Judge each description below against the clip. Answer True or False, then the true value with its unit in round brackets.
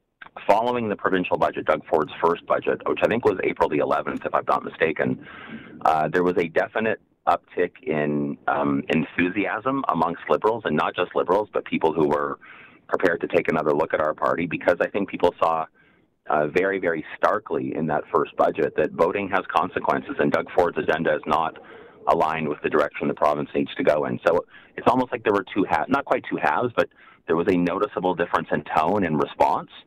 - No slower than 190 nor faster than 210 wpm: True (200 wpm)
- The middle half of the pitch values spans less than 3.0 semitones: False (4.7 semitones)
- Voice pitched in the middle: False (80 Hz)